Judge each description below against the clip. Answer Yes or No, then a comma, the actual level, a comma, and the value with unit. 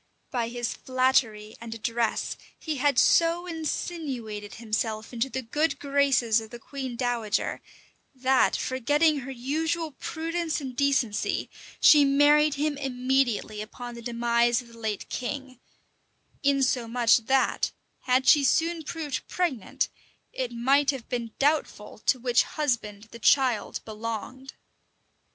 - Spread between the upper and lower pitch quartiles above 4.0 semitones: No, average, 3.5 semitones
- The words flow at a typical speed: No, slow, 130 wpm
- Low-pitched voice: No, very high, 255 Hz